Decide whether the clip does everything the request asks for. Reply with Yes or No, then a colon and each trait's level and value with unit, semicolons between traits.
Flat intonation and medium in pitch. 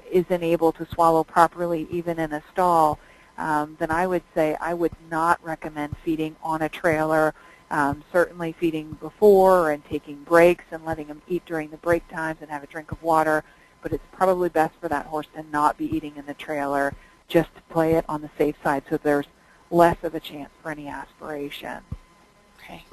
Yes: narrow, 1.9 semitones; medium, 160 Hz